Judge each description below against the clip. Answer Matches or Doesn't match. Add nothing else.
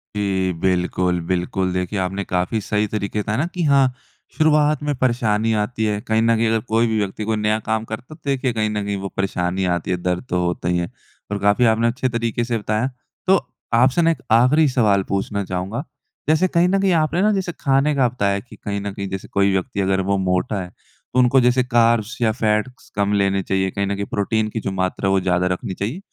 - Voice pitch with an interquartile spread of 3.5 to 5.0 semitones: Matches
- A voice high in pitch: Doesn't match